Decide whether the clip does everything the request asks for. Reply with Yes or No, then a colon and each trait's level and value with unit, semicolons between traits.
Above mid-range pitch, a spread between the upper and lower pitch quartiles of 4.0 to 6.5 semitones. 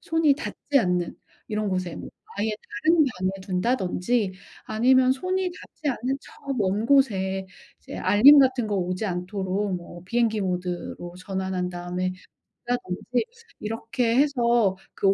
Yes: high, 210 Hz; wide, 5.6 semitones